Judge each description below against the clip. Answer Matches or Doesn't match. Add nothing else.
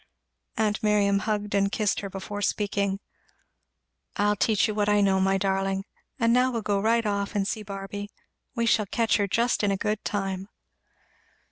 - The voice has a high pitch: Matches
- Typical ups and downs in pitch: Doesn't match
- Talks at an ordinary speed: Matches